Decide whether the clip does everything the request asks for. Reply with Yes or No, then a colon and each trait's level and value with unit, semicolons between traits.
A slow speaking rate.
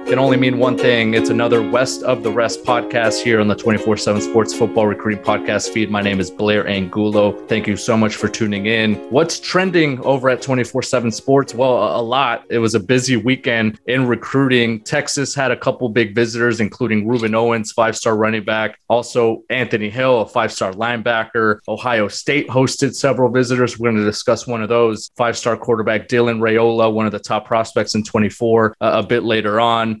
No: average, 200 wpm